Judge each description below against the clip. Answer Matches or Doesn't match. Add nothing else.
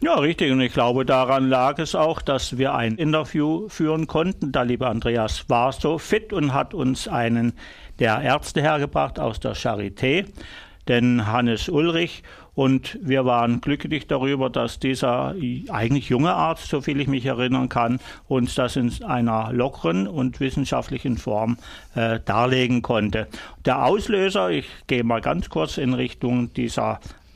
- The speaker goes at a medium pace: Matches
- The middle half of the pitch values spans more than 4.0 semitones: Doesn't match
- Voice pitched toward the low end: Matches